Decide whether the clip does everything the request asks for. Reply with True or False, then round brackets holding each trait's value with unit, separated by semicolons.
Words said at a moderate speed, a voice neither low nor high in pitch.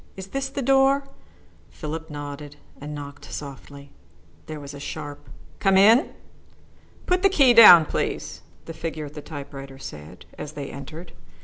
True (150 wpm; 155 Hz)